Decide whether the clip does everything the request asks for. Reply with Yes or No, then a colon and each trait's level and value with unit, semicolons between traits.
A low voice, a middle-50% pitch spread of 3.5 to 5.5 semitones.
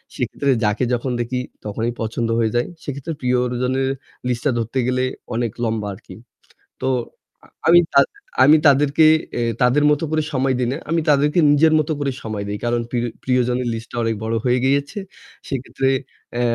No: low, 125 Hz; average, 2.9 semitones